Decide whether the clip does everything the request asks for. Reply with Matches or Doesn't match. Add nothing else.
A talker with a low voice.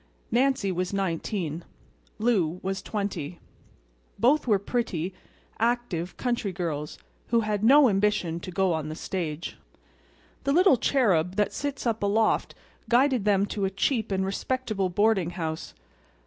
Doesn't match